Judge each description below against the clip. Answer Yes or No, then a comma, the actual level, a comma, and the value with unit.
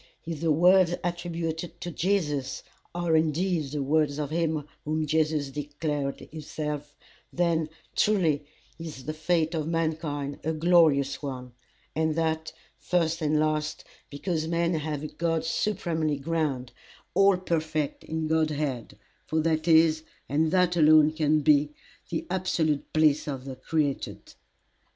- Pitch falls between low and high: Yes, medium, 155 Hz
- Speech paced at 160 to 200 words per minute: No, slow, 135 wpm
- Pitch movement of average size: No, narrow, 1.9 semitones